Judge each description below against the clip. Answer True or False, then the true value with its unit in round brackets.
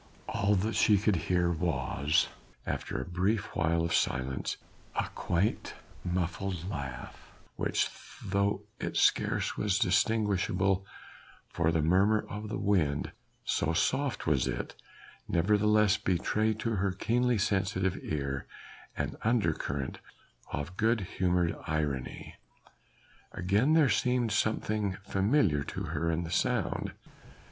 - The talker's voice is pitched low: True (95 Hz)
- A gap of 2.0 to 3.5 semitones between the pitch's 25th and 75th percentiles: False (4.2 semitones)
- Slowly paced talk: True (120 wpm)